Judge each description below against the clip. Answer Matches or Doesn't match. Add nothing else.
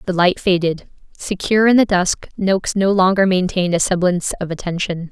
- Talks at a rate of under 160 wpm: Doesn't match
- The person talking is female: Matches